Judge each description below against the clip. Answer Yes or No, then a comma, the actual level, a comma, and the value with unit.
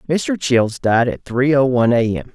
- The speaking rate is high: Yes, fast, 230 wpm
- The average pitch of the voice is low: Yes, low, 130 Hz